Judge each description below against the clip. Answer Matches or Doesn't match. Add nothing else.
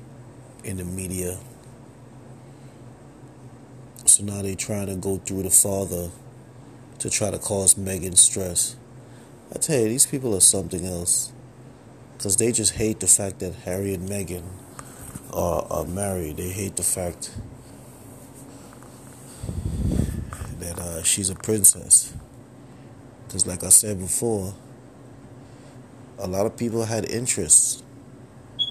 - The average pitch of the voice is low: Matches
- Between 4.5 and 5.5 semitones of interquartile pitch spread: Matches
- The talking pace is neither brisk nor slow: Doesn't match